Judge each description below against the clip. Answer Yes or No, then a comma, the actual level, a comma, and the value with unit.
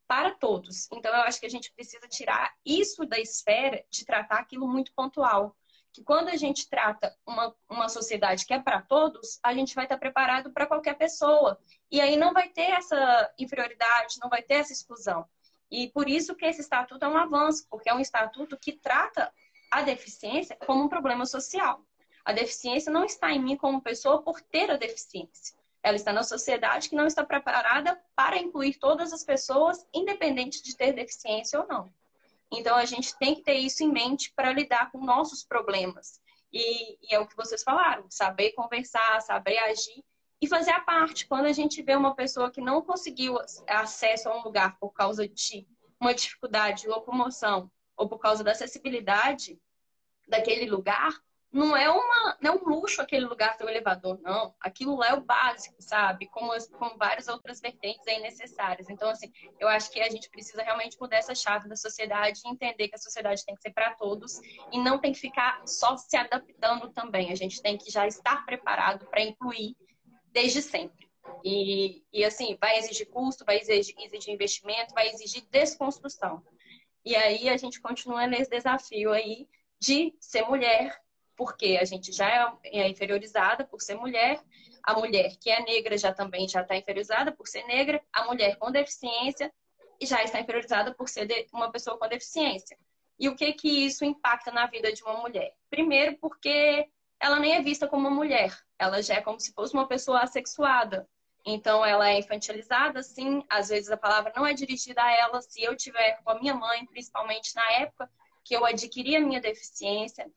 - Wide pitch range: No, average, 4.7 semitones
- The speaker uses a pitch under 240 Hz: No, high, 245 Hz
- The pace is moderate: No, fast, 190 wpm